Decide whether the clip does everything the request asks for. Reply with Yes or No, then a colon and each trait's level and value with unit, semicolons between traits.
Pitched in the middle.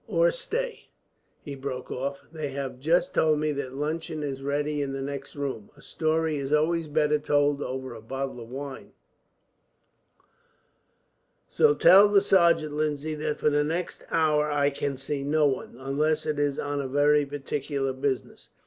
Yes: medium, 145 Hz